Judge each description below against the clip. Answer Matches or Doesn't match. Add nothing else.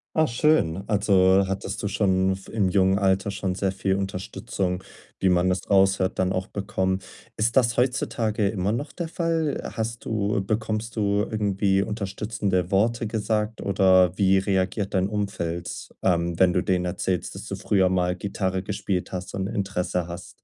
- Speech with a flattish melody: Matches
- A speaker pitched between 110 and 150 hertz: Doesn't match